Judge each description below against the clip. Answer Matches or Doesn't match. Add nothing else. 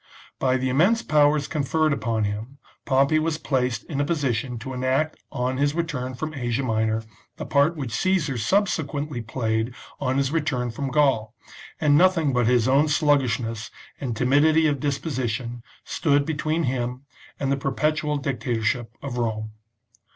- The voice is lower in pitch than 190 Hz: Matches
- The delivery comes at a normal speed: Matches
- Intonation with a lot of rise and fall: Doesn't match